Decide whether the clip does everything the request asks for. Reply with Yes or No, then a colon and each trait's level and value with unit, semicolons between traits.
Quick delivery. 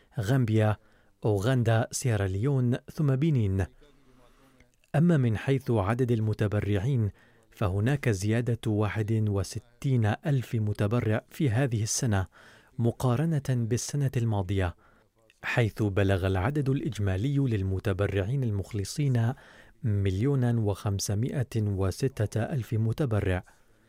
No: average, 85 wpm